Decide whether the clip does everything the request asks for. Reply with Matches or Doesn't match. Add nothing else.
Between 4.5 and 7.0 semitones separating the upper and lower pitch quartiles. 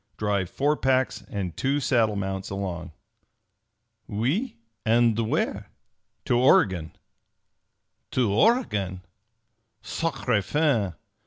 Matches